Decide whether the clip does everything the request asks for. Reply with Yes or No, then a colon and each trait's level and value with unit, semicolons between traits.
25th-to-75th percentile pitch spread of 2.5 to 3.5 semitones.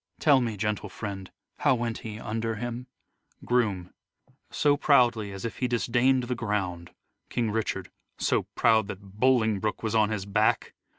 Yes: average, 2.8 semitones